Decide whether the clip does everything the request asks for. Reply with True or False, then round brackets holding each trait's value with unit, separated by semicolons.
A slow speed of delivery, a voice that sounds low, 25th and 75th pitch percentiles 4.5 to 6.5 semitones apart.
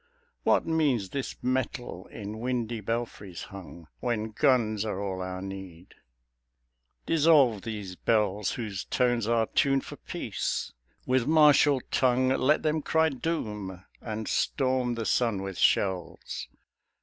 True (125 wpm; 115 Hz; 4.8 semitones)